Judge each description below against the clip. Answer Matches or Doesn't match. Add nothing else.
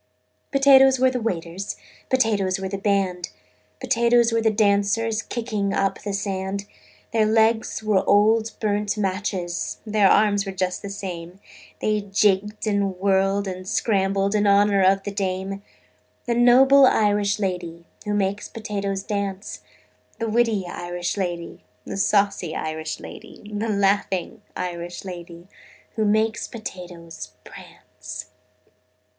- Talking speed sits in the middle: Doesn't match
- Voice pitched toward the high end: Matches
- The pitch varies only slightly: Matches